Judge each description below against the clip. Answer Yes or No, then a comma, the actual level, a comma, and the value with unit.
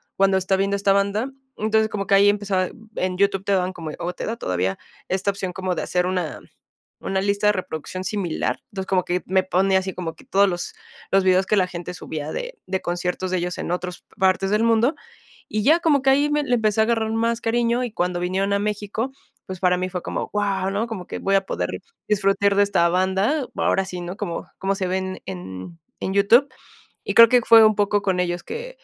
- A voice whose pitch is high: Yes, high, 195 Hz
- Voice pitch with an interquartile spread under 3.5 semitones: Yes, average, 2.7 semitones